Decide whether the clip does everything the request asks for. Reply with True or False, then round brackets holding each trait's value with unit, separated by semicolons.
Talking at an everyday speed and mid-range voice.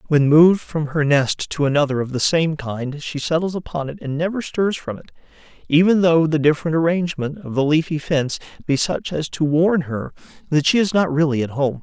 False (215 wpm; 155 Hz)